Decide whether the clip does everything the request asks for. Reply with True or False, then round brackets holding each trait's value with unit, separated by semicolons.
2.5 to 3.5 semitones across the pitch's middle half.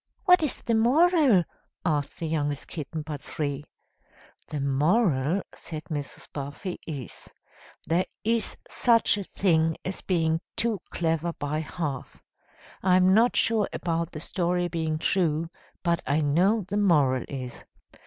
False (4.6 semitones)